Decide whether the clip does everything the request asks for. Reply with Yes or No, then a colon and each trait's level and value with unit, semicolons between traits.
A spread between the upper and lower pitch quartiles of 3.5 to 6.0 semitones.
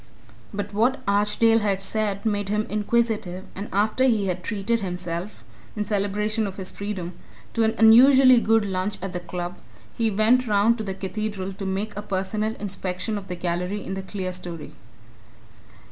No: narrow, 2.4 semitones